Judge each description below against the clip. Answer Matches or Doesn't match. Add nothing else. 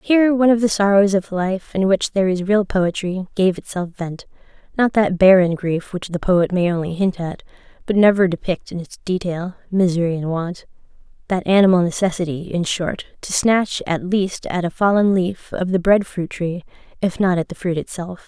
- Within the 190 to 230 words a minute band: Matches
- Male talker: Doesn't match